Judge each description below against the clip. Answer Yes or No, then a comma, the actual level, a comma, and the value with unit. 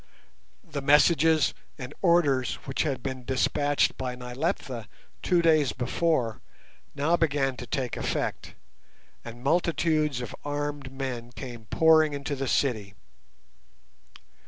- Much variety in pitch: No, average, 3.5 semitones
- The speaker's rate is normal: No, slow, 115 wpm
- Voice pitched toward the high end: No, medium, 140 Hz